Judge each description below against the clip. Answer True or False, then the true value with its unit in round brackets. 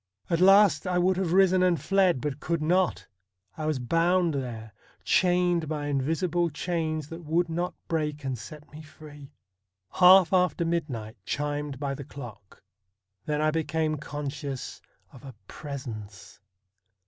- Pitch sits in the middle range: True (155 Hz)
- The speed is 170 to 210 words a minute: False (150 wpm)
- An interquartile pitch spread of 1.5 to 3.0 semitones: False (3.7 semitones)